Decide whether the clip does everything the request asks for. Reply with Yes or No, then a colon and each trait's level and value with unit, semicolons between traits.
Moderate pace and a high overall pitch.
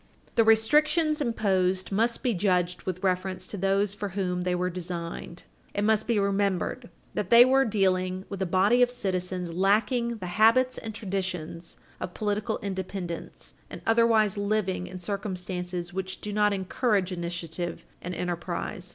Yes: average, 150 wpm; high, 195 Hz